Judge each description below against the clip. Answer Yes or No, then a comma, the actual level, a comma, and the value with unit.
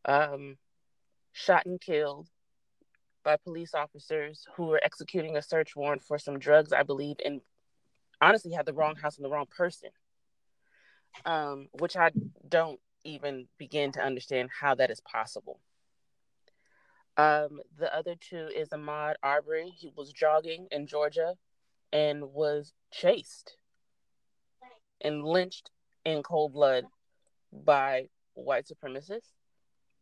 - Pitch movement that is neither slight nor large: No, narrow, 2.3 semitones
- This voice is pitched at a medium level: Yes, medium, 150 Hz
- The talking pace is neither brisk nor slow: No, slow, 125 wpm